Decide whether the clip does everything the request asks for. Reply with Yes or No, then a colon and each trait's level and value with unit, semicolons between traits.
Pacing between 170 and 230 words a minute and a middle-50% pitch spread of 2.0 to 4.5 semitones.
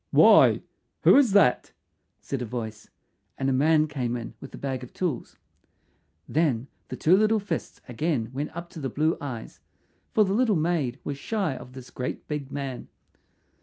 No: average, 175 wpm; average, 5.2 semitones